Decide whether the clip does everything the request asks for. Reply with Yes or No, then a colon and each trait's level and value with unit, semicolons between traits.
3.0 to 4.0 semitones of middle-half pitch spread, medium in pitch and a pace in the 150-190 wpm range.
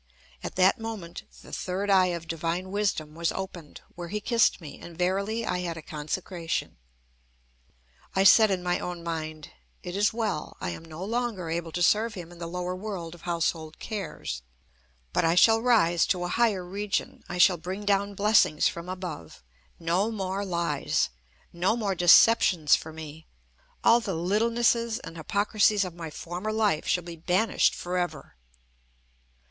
Yes: average, 3.5 semitones; medium, 180 Hz; average, 165 wpm